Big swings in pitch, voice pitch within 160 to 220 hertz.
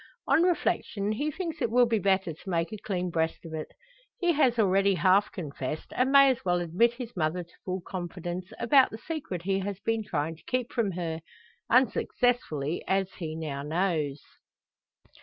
Yes: wide, 6.0 semitones; high, 190 Hz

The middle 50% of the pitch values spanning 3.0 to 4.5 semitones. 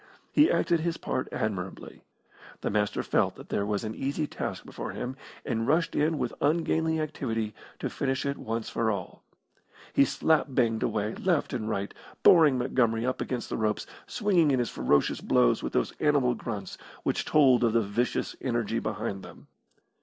No: average, 5.3 semitones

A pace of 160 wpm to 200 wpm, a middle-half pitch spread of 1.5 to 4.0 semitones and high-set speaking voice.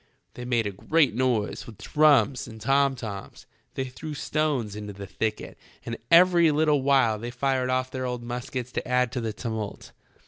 No: average, 180 wpm; average, 3.6 semitones; low, 125 Hz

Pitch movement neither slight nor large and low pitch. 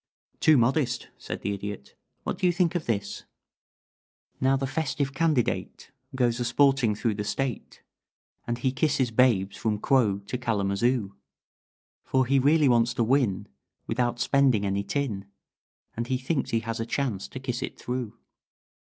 Yes: average, 3.8 semitones; low, 125 Hz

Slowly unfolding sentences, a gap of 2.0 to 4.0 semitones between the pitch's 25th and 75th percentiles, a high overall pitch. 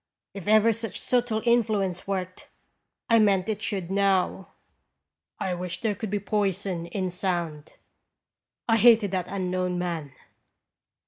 Yes: slow, 130 wpm; average, 3.1 semitones; high, 195 Hz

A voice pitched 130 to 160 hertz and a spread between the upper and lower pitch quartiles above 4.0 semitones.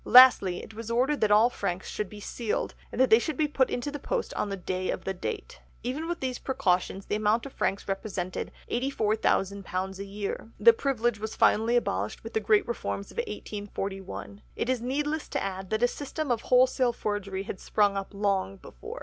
No: high, 215 Hz; average, 4.4 semitones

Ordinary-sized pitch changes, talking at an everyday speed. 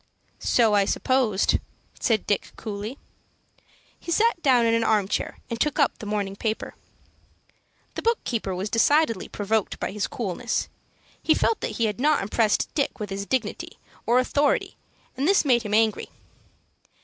Yes: average, 4.2 semitones; average, 160 wpm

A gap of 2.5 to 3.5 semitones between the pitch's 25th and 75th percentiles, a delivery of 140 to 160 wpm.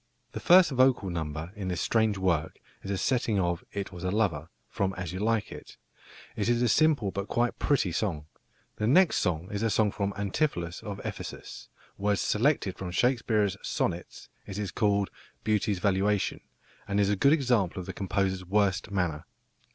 No: average, 3.2 semitones; average, 175 wpm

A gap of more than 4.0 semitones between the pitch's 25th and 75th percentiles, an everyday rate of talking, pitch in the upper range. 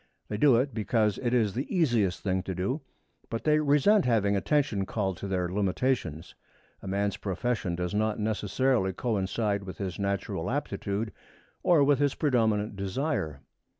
No: average, 4.9 semitones; average, 155 wpm; low, 105 Hz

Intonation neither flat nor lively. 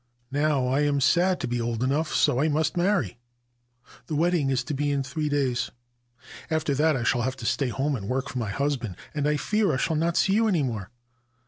Yes: average, 3.7 semitones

